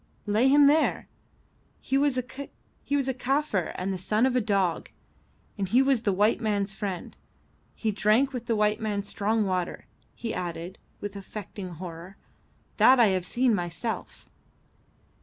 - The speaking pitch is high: Yes, high, 210 Hz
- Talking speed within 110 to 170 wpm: Yes, average, 145 wpm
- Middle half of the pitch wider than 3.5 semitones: Yes, average, 4.7 semitones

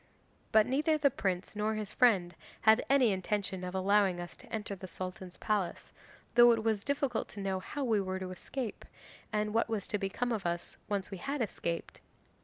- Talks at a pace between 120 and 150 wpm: No, average, 200 wpm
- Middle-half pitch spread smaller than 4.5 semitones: Yes, average, 3.5 semitones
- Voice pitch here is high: Yes, high, 210 Hz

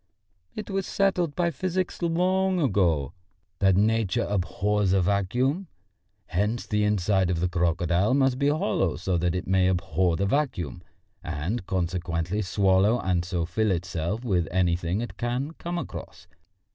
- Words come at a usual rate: Yes, average, 145 wpm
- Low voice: Yes, low, 100 Hz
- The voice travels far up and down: Yes, wide, 6.5 semitones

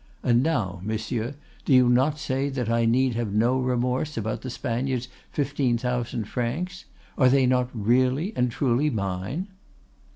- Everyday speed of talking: Yes, average, 155 wpm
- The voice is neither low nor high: No, low, 125 Hz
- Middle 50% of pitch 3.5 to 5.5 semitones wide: No, narrow, 2.4 semitones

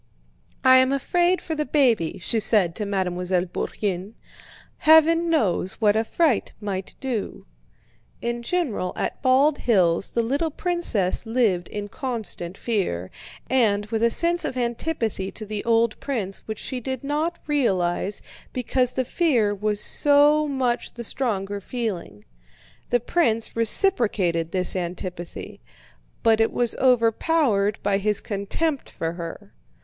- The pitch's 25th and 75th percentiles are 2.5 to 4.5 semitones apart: No, average, 5.3 semitones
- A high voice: Yes, high, 225 Hz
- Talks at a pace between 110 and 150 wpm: Yes, slow, 135 wpm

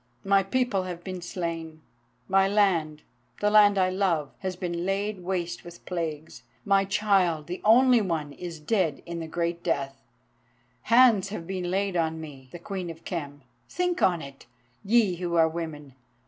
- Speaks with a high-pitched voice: No, medium, 175 Hz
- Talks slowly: No, average, 160 wpm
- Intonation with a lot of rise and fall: No, average, 3.4 semitones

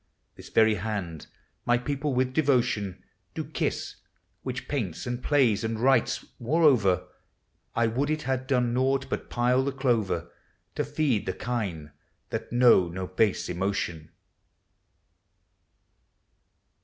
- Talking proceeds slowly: Yes, slow, 130 wpm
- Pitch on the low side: Yes, low, 120 Hz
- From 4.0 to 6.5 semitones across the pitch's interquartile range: Yes, average, 5.1 semitones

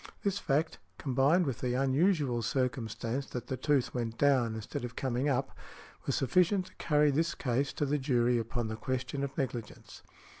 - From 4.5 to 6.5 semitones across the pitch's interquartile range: No, average, 3.2 semitones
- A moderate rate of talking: Yes, average, 175 wpm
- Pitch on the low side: Yes, low, 130 Hz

